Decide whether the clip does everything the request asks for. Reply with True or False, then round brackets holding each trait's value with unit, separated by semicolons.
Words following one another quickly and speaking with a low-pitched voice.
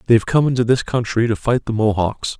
True (250 wpm; 115 Hz)